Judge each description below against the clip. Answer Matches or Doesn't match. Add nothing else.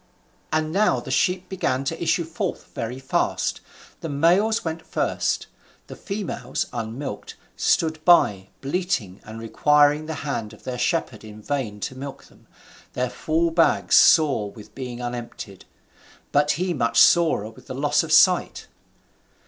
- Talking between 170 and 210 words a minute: Doesn't match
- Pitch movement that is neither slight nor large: Doesn't match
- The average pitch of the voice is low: Doesn't match